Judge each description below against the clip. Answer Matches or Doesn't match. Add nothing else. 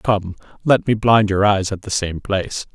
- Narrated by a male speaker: Matches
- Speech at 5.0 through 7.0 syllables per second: Doesn't match